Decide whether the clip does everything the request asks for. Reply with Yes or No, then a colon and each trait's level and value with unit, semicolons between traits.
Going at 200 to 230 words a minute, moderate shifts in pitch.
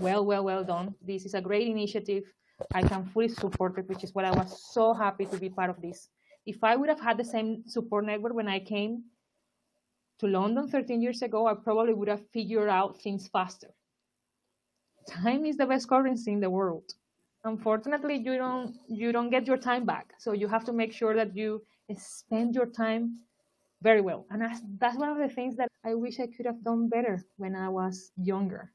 Yes: fast, 205 wpm; average, 3.3 semitones